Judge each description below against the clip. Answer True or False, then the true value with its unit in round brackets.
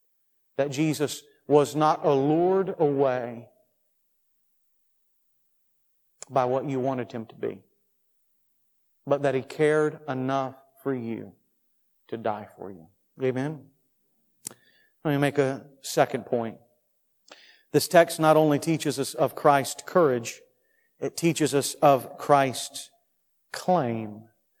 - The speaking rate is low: True (110 wpm)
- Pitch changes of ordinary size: True (3.0 semitones)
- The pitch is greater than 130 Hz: True (140 Hz)